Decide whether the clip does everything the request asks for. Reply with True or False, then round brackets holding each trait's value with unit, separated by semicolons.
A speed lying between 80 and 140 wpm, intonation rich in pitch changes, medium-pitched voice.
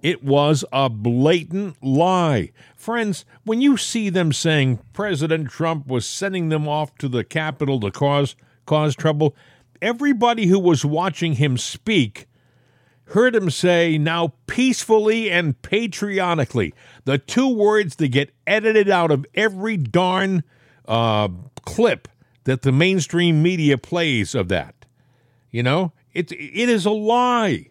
True (135 wpm; 6.4 semitones; 155 Hz)